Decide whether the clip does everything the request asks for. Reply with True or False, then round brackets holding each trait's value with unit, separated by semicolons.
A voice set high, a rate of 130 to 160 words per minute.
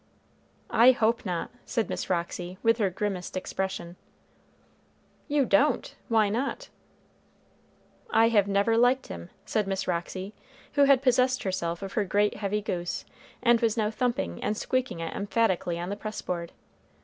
True (205 Hz; 150 wpm)